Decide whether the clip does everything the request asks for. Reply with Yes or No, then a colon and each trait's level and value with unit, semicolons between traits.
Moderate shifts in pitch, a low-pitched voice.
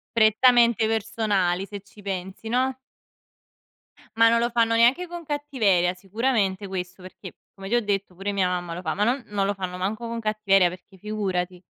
No: average, 3.6 semitones; high, 205 Hz